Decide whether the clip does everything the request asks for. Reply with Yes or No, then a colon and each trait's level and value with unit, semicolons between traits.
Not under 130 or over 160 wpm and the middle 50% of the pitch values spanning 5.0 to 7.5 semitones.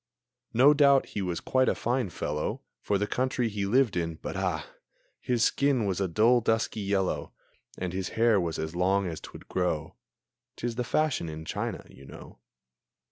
No: average, 180 wpm; wide, 5.5 semitones